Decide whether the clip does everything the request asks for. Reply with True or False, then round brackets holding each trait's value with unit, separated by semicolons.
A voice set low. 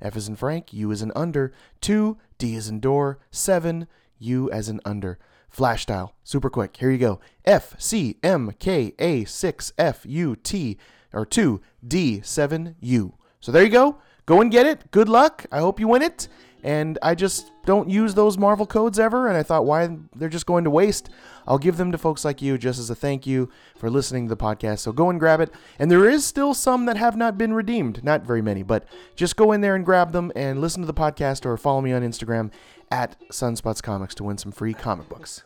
False (145 Hz)